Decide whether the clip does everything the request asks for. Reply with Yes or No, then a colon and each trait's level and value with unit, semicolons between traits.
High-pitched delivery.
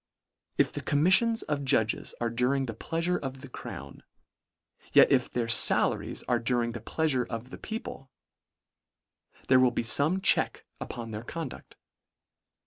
No: low, 130 Hz